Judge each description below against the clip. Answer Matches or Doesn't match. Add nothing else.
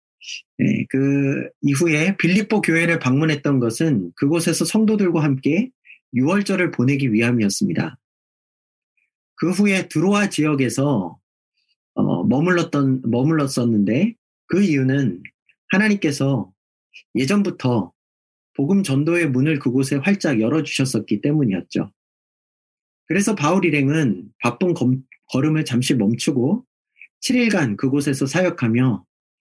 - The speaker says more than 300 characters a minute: Doesn't match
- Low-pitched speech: Doesn't match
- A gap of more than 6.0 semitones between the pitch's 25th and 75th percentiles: Doesn't match